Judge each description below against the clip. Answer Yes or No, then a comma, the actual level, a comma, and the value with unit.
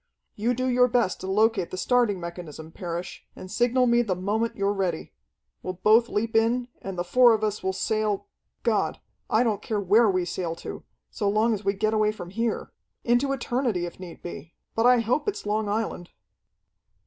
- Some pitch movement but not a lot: Yes, average, 4.0 semitones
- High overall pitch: Yes, high, 215 Hz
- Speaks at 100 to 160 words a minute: No, average, 195 wpm